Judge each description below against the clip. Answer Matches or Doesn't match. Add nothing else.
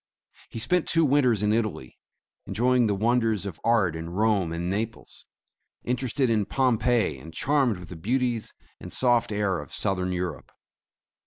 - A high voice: Doesn't match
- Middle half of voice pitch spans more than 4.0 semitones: Matches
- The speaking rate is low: Doesn't match